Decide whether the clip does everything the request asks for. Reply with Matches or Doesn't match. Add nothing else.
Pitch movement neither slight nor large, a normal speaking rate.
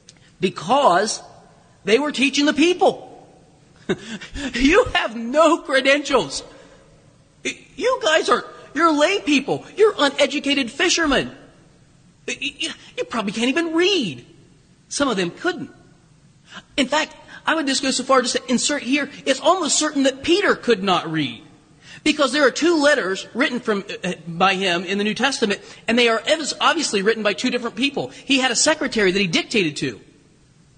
Doesn't match